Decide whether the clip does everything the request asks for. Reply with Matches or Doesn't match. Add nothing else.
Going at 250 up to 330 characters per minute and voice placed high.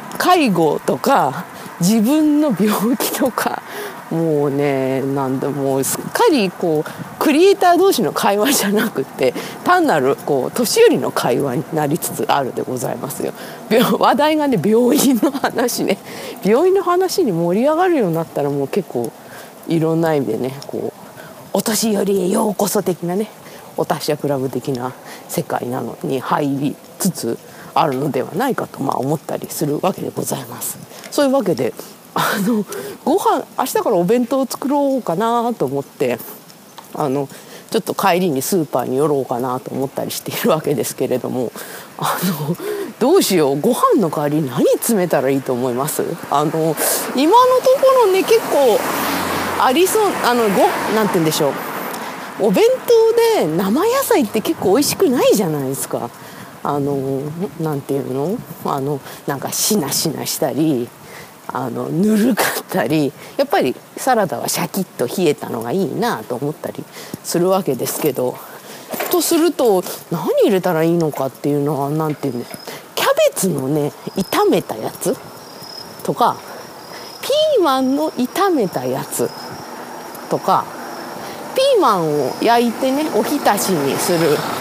Matches